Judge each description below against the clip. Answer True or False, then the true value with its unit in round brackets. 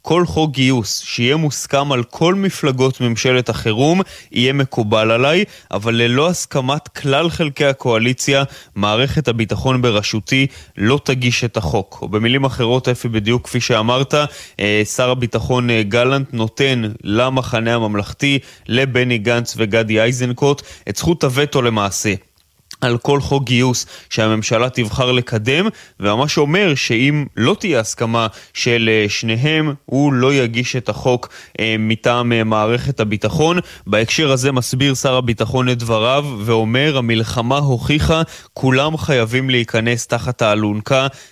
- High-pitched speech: False (125 Hz)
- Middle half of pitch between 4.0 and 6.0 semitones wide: False (3.4 semitones)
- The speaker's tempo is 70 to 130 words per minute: True (125 wpm)